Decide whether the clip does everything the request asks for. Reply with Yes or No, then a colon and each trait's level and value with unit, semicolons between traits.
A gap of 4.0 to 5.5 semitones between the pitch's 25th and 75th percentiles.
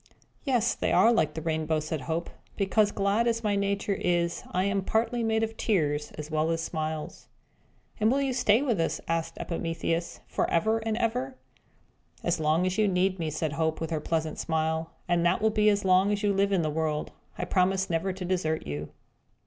Yes: average, 4.8 semitones